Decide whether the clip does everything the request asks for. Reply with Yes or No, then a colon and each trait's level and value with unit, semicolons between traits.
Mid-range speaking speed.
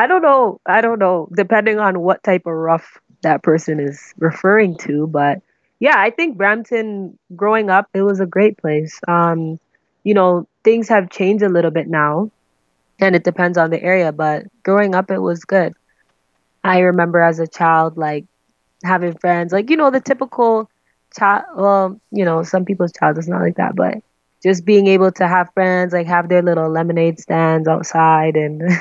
Yes: average, 185 wpm